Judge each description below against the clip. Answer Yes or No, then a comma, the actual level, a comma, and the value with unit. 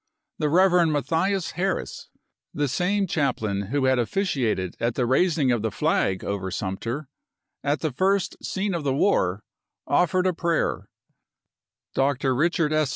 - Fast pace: No, average, 150 wpm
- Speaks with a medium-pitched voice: Yes, medium, 145 Hz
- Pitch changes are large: Yes, wide, 6.8 semitones